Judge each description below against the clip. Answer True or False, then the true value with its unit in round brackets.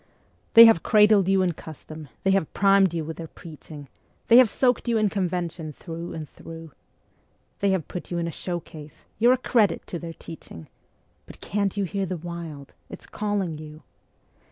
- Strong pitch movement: False (3.7 semitones)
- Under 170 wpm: False (180 wpm)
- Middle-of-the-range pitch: True (175 Hz)